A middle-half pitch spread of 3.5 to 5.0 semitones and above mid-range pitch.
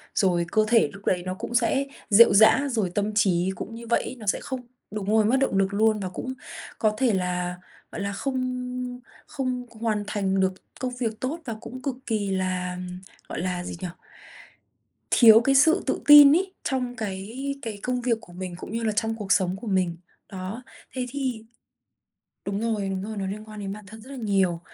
Yes: average, 4.5 semitones; high, 215 Hz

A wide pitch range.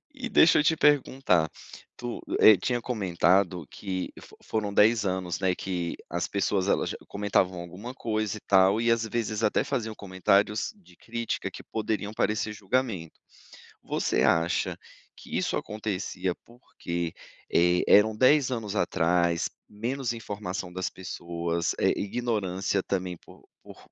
No: average, 3.9 semitones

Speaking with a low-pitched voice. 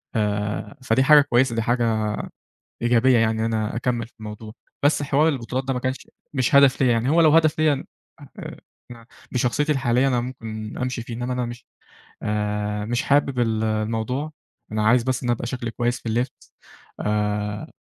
Yes: low, 120 Hz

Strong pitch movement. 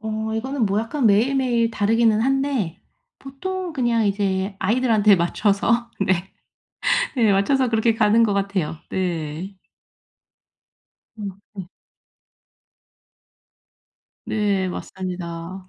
No: average, 3.7 semitones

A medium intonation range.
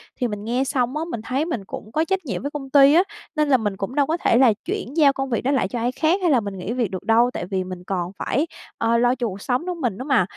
Yes: average, 5.0 semitones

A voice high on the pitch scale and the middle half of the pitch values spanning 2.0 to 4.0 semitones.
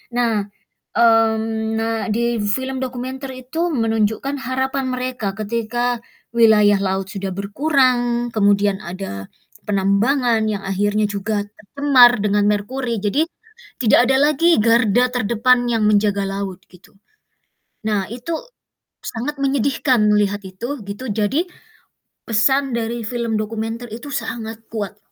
Yes: high, 225 Hz; average, 3.4 semitones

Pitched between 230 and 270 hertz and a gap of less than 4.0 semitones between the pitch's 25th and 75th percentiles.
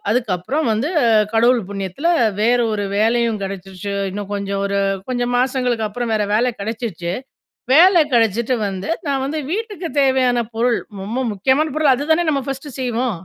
No: high, 240 Hz; average, 4.5 semitones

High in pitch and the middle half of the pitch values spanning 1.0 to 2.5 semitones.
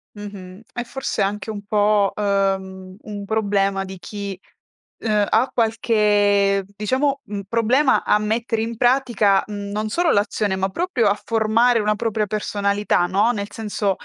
Yes: high, 210 Hz; narrow, 2.1 semitones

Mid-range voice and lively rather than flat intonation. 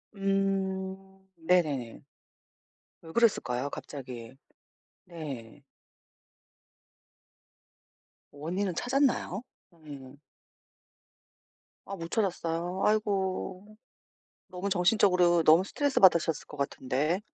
No: medium, 180 Hz; average, 4.5 semitones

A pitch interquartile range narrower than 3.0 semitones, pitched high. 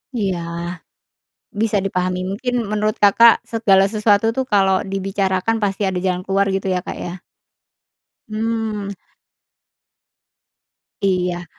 Yes: narrow, 2.4 semitones; high, 195 Hz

